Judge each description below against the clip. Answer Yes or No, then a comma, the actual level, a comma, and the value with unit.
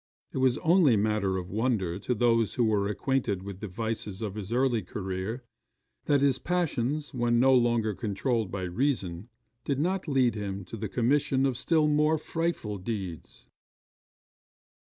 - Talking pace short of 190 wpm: Yes, average, 155 wpm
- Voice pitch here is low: Yes, low, 115 Hz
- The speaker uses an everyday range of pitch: Yes, average, 5.0 semitones